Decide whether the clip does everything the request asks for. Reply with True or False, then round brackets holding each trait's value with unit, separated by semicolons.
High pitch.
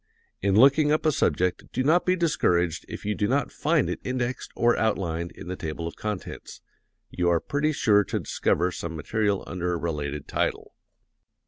False (100 Hz)